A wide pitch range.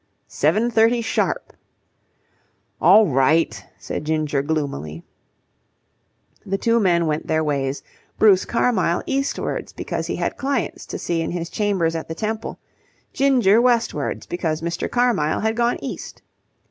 Yes: wide, 6.6 semitones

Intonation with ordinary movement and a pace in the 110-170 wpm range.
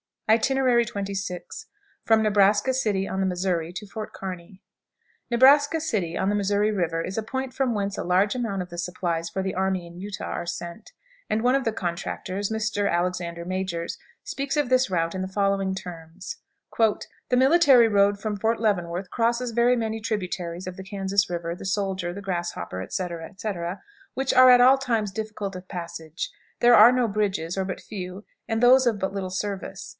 No: average, 3.7 semitones; average, 180 wpm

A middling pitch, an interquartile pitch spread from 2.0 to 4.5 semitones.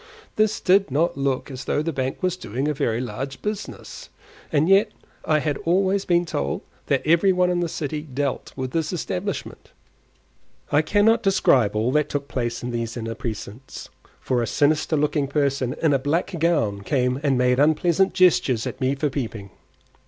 No: medium, 145 Hz; average, 5.2 semitones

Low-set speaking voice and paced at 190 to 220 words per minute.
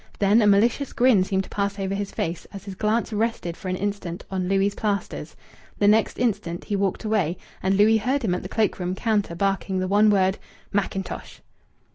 No: high, 200 Hz; average, 200 wpm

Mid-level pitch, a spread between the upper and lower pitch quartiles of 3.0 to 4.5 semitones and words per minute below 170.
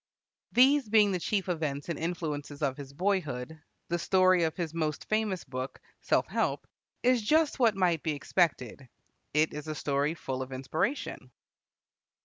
No: medium, 165 Hz; average, 5.2 semitones; average, 155 wpm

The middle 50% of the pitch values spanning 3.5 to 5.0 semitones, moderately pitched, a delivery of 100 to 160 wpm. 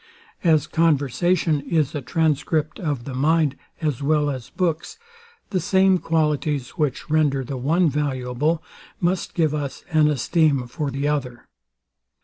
No: average, 2.8 semitones; medium, 150 Hz; slow, 135 wpm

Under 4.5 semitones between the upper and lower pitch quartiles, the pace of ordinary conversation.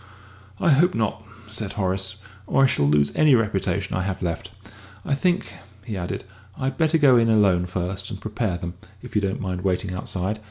No: average, 4.9 semitones; average, 190 wpm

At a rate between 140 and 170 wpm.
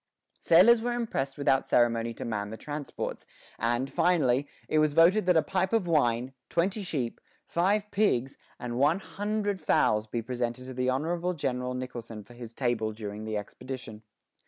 Yes: average, 165 wpm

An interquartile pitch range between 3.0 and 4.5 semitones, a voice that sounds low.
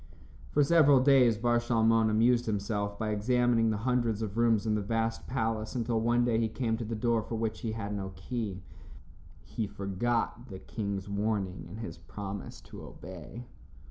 No: narrow, 2.5 semitones; low, 110 Hz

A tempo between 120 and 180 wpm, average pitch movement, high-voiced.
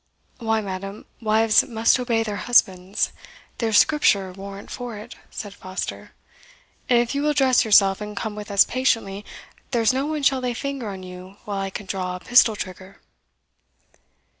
Yes: average, 165 wpm; average, 3.8 semitones; high, 215 Hz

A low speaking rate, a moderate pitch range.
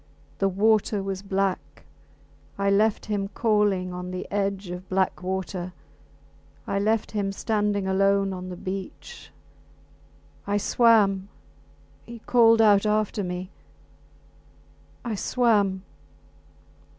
No: slow, 110 wpm; narrow, 1.9 semitones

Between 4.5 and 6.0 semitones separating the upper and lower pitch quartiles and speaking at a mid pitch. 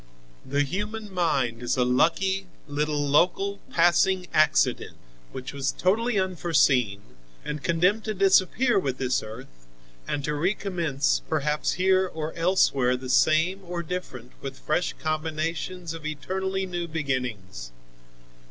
Yes: average, 5.3 semitones; medium, 160 Hz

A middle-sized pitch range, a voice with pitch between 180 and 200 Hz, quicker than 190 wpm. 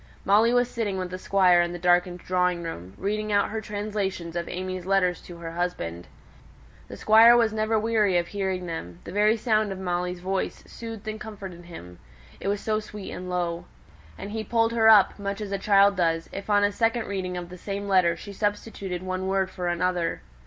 Yes: average, 3.0 semitones; high, 190 Hz; fast, 205 wpm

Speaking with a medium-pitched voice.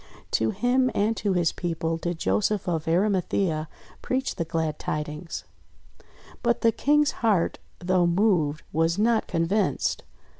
Yes: medium, 180 Hz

